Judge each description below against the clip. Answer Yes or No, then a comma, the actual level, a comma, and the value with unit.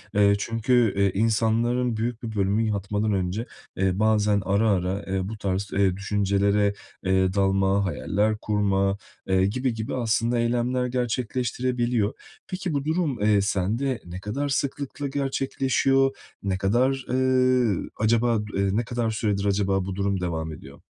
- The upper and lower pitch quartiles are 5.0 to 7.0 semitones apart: No, average, 3.9 semitones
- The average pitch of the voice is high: No, low, 105 Hz